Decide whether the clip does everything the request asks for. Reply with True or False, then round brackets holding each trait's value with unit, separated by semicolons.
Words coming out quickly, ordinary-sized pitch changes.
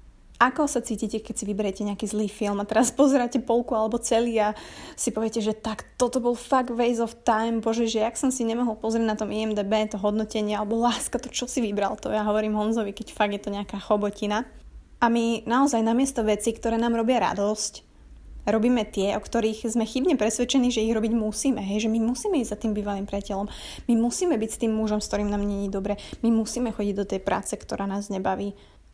False (215 wpm; 2.3 semitones)